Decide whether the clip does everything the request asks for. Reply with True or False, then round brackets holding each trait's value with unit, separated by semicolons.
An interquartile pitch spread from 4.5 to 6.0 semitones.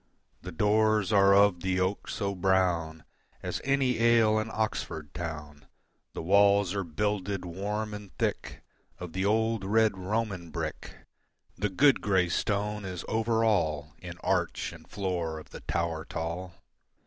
False (3.6 semitones)